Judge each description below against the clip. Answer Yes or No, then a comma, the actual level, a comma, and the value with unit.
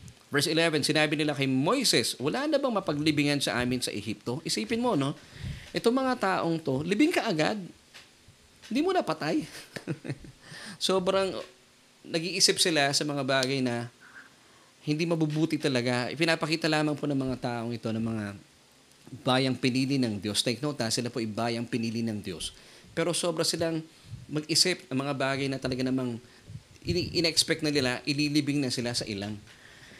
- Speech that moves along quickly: Yes, fast, 160 wpm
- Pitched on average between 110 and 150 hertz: Yes, medium, 140 Hz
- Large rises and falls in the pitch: No, average, 4.8 semitones